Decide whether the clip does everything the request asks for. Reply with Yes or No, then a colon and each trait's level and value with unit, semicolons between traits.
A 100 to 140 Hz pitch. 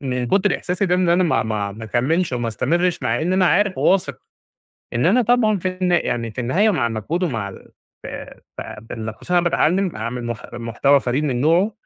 No: medium, 155 Hz